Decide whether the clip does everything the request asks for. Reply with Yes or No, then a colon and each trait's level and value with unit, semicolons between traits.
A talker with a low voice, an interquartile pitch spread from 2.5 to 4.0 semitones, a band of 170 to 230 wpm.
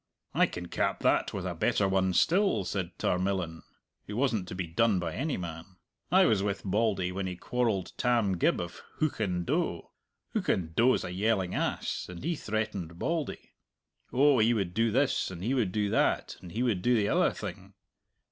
No: low, 100 Hz; average, 4.5 semitones; average, 185 wpm